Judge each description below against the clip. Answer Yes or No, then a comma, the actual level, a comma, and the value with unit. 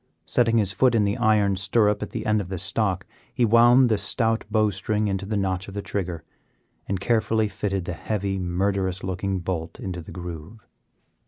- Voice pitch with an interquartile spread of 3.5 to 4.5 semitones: No, narrow, 2.6 semitones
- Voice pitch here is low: Yes, low, 100 Hz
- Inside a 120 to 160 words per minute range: No, average, 190 wpm